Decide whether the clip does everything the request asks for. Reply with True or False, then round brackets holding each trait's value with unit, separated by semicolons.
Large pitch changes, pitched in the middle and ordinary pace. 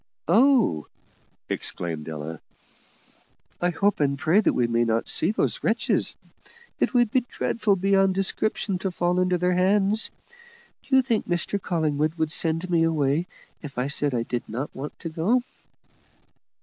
True (5.8 semitones; 175 Hz; 155 wpm)